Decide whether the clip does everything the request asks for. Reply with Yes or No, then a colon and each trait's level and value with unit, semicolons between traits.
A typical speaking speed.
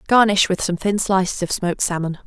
No: fast, 210 wpm